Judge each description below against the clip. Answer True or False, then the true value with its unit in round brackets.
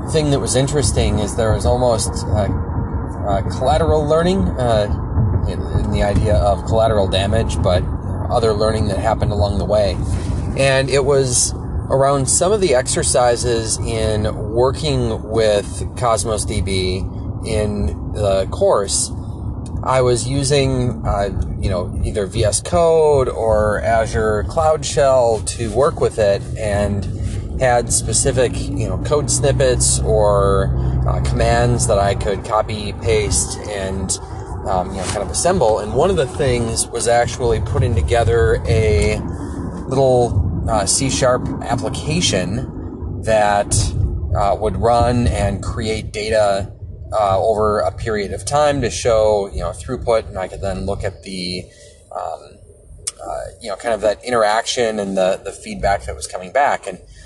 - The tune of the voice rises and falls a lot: False (3.3 semitones)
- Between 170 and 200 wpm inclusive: False (145 wpm)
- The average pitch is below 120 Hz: True (105 Hz)